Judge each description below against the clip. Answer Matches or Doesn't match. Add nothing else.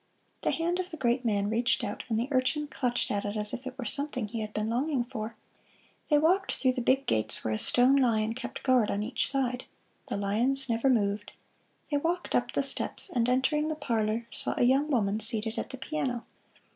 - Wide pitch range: Doesn't match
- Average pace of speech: Doesn't match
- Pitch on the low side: Doesn't match